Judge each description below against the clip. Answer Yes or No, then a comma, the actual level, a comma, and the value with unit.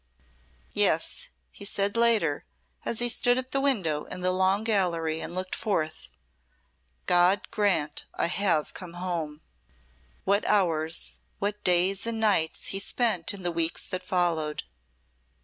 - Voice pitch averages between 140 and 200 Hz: Yes, medium, 185 Hz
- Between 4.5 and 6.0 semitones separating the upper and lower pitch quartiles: No, average, 3.7 semitones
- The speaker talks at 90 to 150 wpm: Yes, average, 140 wpm